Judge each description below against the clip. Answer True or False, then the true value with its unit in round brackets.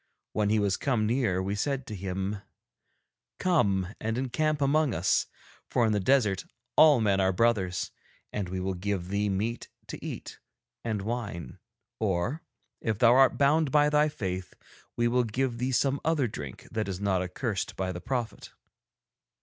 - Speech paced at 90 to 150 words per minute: False (165 wpm)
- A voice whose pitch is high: False (110 Hz)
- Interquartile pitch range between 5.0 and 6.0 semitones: True (5.4 semitones)